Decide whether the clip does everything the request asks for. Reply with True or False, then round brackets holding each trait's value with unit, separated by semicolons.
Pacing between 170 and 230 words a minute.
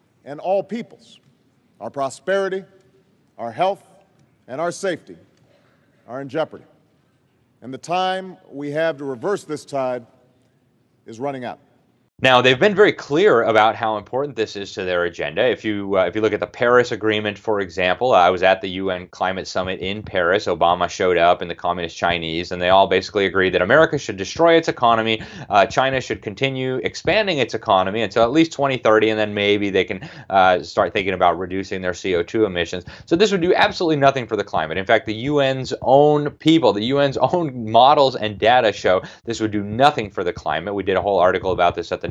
True (200 wpm)